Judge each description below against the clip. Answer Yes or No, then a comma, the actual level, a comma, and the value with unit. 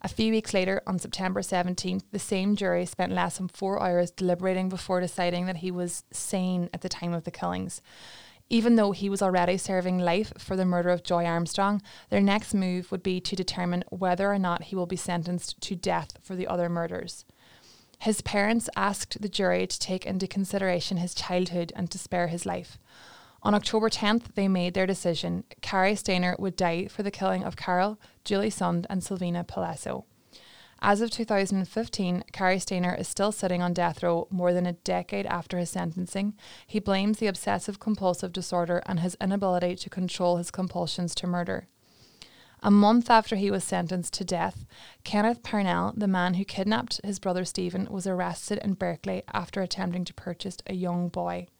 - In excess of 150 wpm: Yes, average, 185 wpm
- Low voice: No, medium, 185 Hz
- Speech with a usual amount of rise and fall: No, narrow, 2.0 semitones